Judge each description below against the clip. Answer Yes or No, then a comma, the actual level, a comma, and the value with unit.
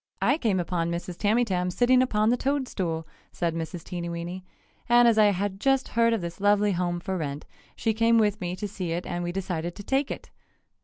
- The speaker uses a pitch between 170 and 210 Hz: Yes, high, 190 Hz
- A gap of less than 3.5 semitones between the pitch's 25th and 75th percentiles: No, average, 4.6 semitones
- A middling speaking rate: No, fast, 210 wpm